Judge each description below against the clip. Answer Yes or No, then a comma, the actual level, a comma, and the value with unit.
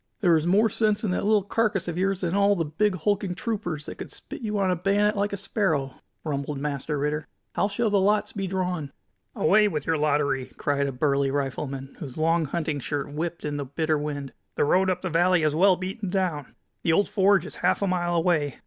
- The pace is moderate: No, fast, 225 wpm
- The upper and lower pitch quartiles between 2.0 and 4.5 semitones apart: No, average, 5.1 semitones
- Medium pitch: Yes, medium, 175 Hz